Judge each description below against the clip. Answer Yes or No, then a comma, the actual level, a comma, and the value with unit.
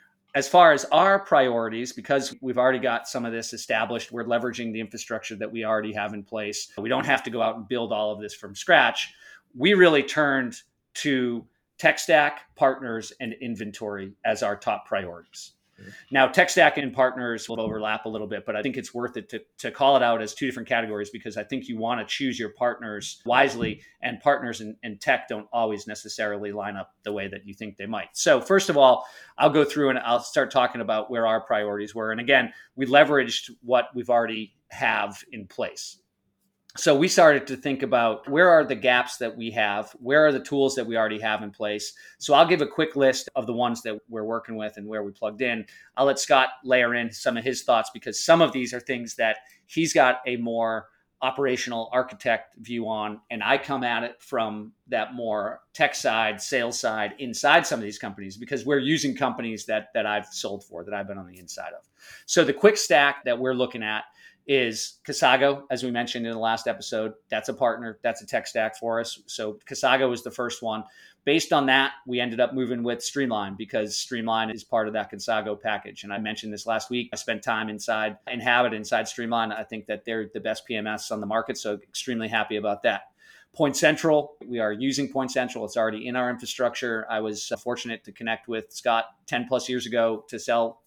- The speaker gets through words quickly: Yes, fast, 215 wpm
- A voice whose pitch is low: Yes, low, 115 Hz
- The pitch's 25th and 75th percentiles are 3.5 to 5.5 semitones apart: No, average, 2.9 semitones